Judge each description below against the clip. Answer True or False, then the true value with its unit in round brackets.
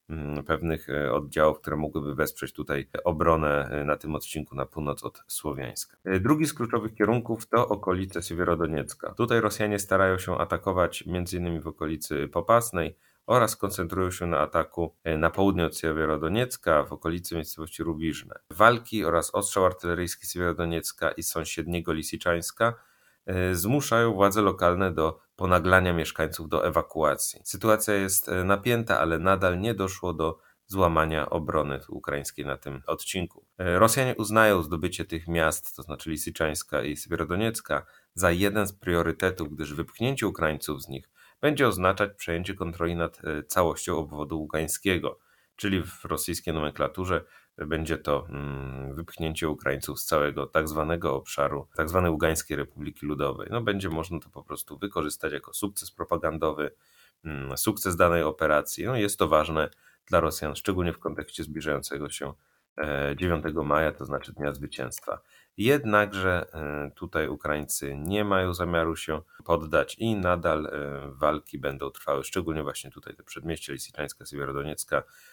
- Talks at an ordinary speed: True (135 wpm)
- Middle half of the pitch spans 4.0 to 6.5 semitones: False (3.6 semitones)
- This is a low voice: True (85 Hz)